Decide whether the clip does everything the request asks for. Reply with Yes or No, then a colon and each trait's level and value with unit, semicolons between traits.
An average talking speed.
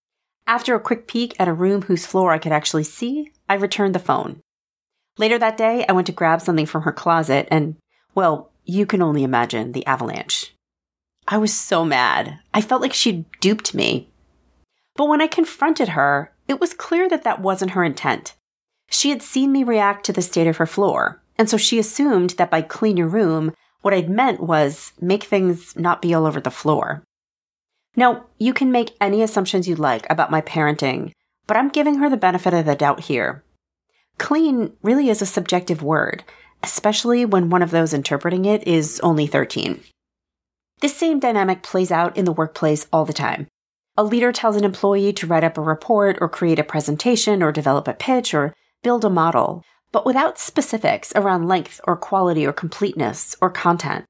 Yes: average, 190 wpm